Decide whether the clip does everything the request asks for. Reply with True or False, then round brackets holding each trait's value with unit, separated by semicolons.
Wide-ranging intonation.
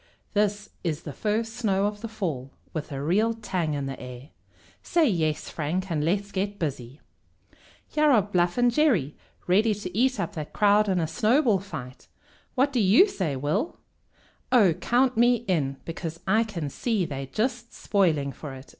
True (6.5 semitones)